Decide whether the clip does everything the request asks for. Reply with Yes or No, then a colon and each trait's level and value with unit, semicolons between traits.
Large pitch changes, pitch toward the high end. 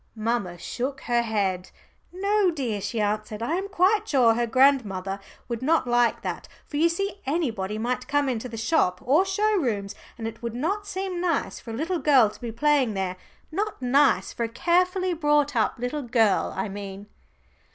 Yes: wide, 7.0 semitones; very high, 250 Hz